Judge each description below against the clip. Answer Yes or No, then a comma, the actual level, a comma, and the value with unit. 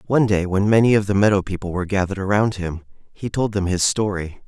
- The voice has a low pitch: Yes, low, 100 Hz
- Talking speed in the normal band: No, fast, 230 wpm